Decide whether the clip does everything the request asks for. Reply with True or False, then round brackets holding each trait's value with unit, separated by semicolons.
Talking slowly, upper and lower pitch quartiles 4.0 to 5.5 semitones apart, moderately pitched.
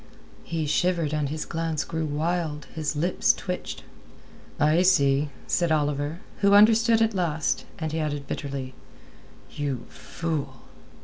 False (130 wpm; 3.0 semitones; 155 Hz)